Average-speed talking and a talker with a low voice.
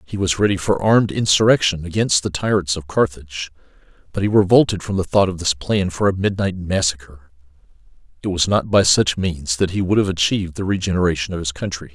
Yes: average, 195 wpm; very low, 90 Hz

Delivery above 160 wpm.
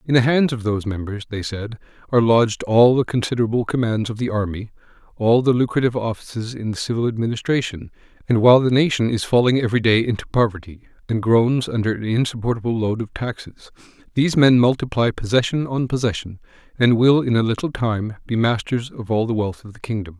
Yes: average, 190 wpm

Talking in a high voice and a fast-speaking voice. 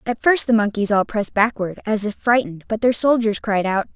Yes: high, 215 Hz; fast, 225 wpm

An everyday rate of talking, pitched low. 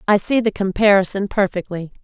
No: average, 150 wpm; high, 200 Hz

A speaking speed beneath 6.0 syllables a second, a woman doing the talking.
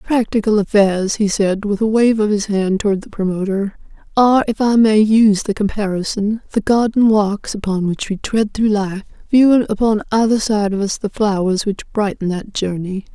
Yes: 5.1 syllables/s; female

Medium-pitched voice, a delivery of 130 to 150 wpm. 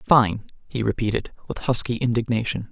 No: low, 115 Hz; slow, 135 wpm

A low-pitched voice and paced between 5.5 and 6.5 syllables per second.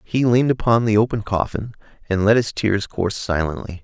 Yes: low, 105 Hz; 5.6 syllables/s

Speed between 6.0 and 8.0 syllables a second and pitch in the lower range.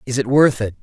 Yes: 6.2 syllables/s; low, 125 Hz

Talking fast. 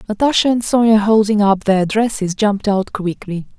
No: average, 165 wpm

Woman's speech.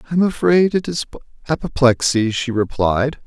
No: male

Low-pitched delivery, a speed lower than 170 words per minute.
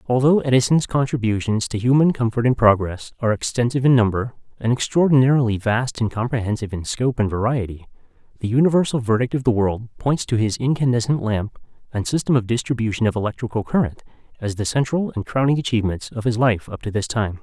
No: low, 120 Hz; average, 180 wpm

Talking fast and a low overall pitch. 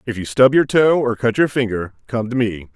Yes: fast, 260 wpm; low, 115 Hz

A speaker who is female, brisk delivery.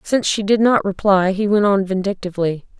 No: female; average, 195 wpm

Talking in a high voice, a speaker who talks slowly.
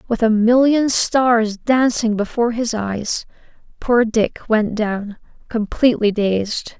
Yes: high, 225 Hz; slow, 125 wpm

